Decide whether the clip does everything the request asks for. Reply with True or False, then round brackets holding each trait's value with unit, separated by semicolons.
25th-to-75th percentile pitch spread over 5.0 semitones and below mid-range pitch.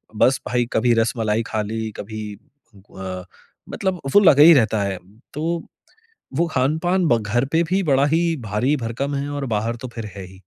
True (5.6 semitones; 125 Hz)